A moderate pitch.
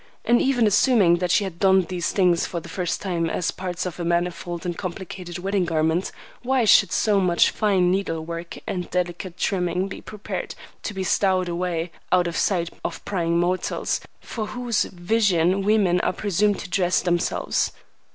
Yes: medium, 180 Hz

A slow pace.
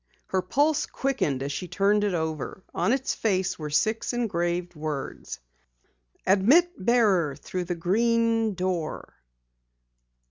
Yes: slow, 120 wpm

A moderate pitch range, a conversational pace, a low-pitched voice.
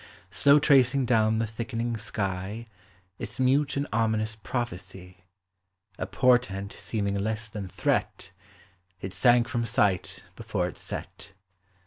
No: average, 3.5 semitones; slow, 120 wpm; low, 110 Hz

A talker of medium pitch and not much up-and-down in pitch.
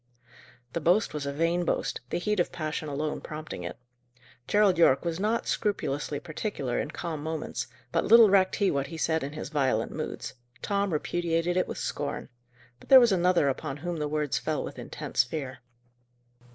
No: medium, 160 Hz; average, 3.8 semitones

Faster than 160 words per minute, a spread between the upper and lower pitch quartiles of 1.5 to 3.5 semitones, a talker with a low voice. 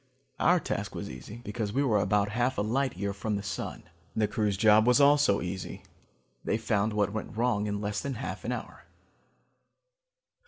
Yes: average, 185 wpm; average, 2.8 semitones; low, 105 Hz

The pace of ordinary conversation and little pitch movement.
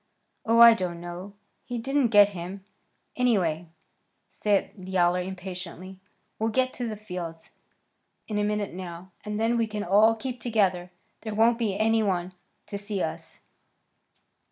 No: average, 150 wpm; average, 3.6 semitones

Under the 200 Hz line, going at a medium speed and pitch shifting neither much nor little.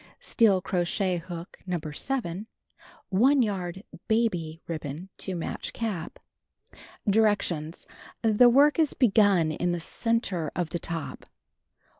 No: medium, 185 Hz; slow, 115 wpm; average, 4.8 semitones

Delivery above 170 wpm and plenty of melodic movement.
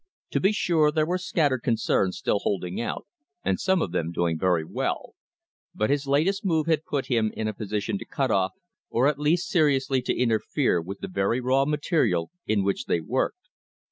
Yes: average, 195 wpm; wide, 7.6 semitones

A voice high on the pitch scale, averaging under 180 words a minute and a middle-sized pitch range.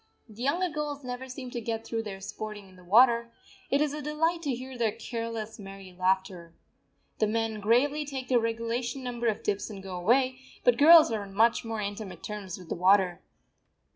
No: high, 230 Hz; average, 200 wpm; average, 4.1 semitones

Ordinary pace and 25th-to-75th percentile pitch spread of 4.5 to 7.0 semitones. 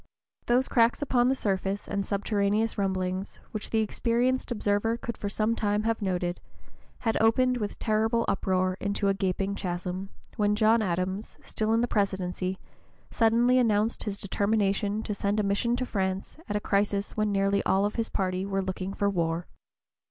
No: average, 165 wpm; narrow, 2.6 semitones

